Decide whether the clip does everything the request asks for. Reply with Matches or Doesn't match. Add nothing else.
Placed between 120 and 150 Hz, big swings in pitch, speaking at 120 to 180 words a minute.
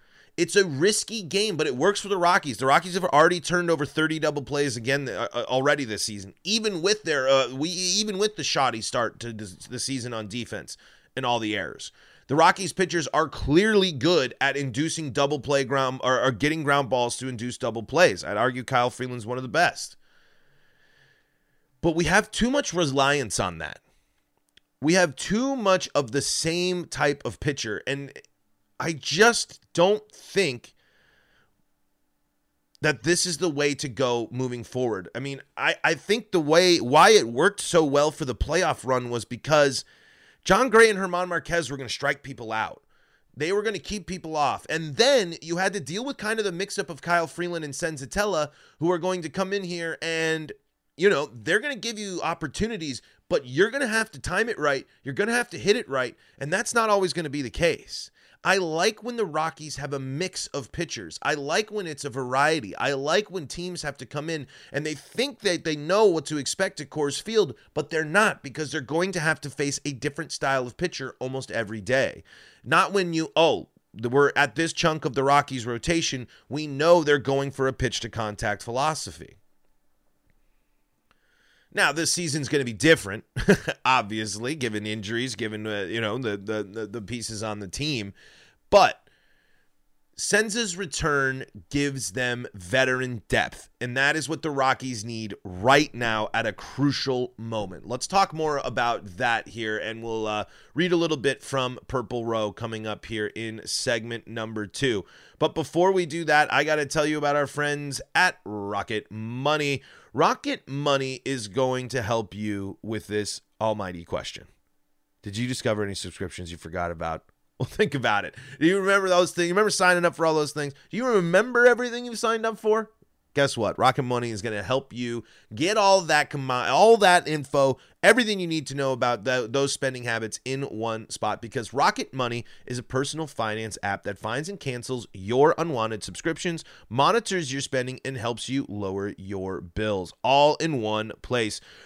Doesn't match